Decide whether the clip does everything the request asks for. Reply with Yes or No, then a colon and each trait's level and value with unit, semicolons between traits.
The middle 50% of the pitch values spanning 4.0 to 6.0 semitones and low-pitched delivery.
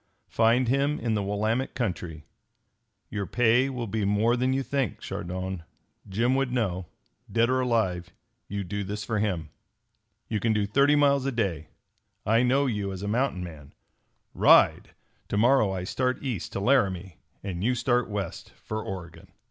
Yes: average, 4.8 semitones; low, 110 Hz